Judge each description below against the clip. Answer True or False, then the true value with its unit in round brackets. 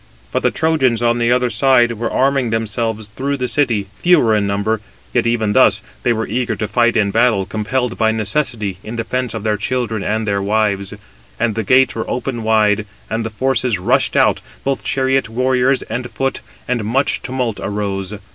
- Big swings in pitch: False (3.0 semitones)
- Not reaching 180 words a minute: False (185 wpm)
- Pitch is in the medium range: False (115 Hz)